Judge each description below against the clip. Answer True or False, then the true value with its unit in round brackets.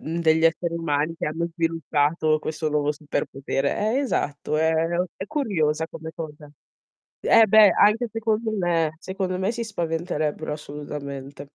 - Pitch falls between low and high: True (160 Hz)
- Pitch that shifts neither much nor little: True (4.0 semitones)